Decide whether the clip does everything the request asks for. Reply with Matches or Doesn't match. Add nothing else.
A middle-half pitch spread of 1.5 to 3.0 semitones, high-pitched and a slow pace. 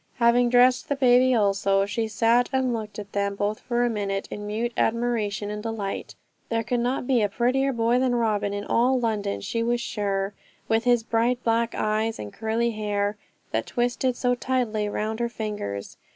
Doesn't match